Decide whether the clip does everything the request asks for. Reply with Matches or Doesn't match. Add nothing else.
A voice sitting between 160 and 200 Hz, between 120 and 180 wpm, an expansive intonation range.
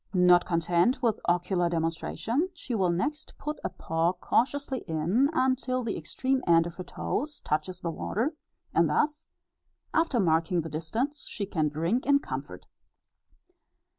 Matches